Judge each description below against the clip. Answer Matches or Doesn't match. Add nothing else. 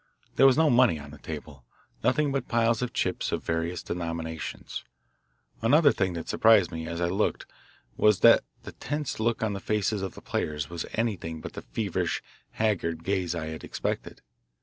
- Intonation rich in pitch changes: Matches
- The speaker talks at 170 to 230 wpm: Matches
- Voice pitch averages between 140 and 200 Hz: Doesn't match